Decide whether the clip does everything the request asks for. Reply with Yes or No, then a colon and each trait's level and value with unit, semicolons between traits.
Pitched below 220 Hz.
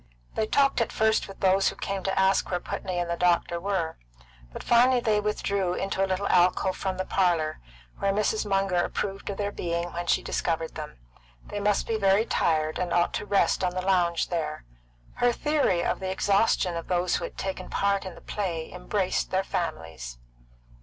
Yes: high, 190 Hz